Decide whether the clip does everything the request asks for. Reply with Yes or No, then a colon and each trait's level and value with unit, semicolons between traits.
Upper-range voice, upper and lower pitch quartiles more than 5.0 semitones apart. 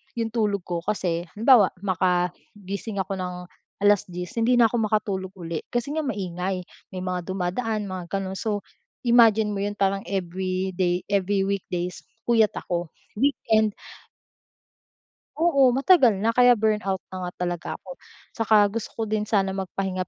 No: high, 195 Hz; average, 3.3 semitones